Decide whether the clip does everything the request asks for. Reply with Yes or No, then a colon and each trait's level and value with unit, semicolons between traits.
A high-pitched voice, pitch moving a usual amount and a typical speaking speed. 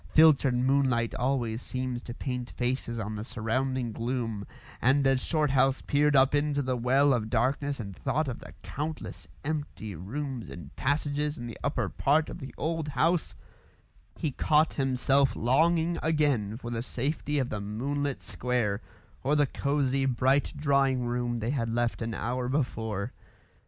No: low, 130 Hz; average, 3.4 semitones; average, 155 wpm